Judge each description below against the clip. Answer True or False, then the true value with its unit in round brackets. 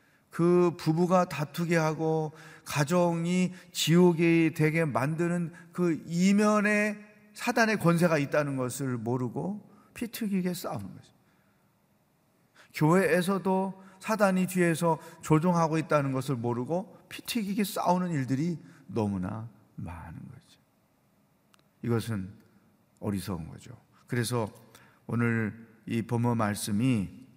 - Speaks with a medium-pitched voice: True (165 Hz)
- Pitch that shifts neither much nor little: False (6.6 semitones)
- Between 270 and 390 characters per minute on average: False (235 characters per minute)